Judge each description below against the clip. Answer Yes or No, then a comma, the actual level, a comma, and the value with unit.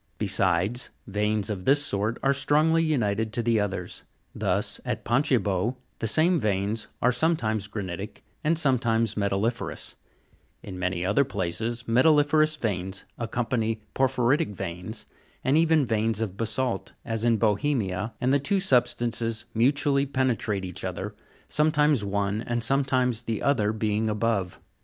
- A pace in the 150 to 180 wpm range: No, average, 140 wpm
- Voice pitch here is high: No, low, 115 Hz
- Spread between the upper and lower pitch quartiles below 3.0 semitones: No, average, 4.7 semitones